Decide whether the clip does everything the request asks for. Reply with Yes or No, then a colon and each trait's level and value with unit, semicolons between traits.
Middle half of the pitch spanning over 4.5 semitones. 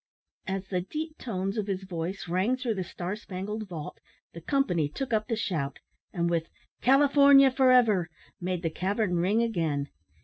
Yes: average, 5.1 semitones